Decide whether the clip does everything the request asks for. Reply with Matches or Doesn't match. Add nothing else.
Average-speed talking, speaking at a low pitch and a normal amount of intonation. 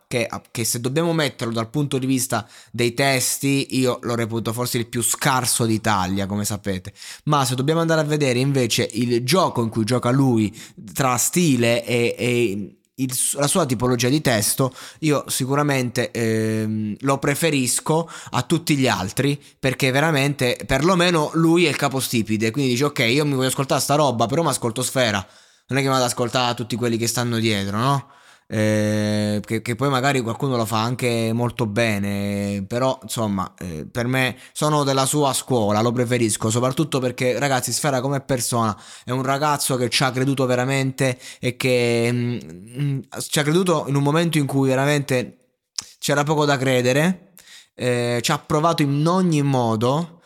Doesn't match